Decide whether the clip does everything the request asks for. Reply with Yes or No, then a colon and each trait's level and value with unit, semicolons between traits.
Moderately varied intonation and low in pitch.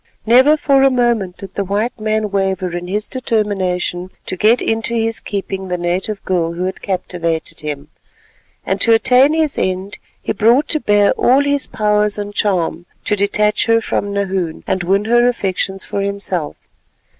No: average, 3.5 semitones; high, 200 Hz